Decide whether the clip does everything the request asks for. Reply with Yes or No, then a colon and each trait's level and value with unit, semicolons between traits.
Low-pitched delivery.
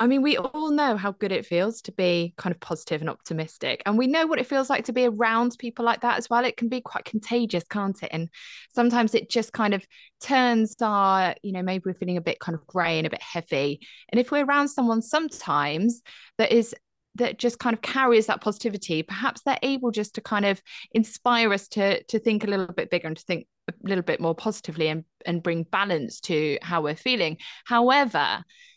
No: high, 215 Hz